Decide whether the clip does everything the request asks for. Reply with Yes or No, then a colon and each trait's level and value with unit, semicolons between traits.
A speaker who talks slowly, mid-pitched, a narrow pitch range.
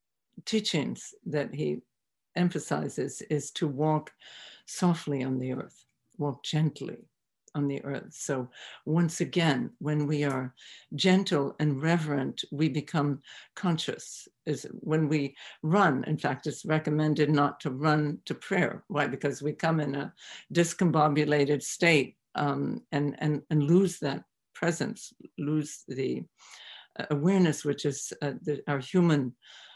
Yes: slow, 125 wpm; medium, 150 Hz; narrow, 2.3 semitones